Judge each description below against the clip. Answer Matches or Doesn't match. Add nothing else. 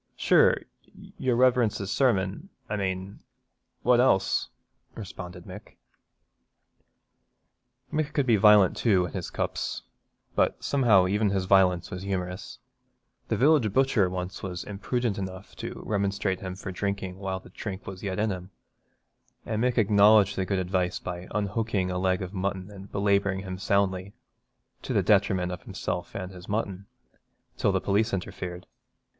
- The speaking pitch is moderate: Doesn't match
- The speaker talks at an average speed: Matches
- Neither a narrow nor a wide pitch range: Doesn't match